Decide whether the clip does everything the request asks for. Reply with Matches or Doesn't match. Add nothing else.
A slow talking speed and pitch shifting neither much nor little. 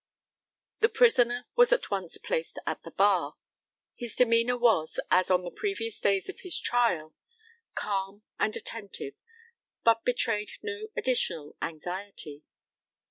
Matches